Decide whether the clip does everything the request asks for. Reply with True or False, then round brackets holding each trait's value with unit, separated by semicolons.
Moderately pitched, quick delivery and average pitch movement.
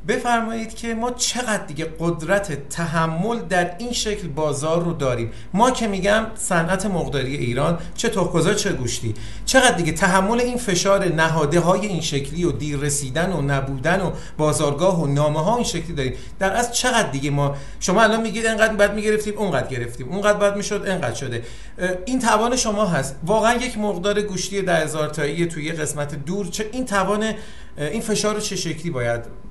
False (180 Hz; 170 wpm; 6.1 semitones)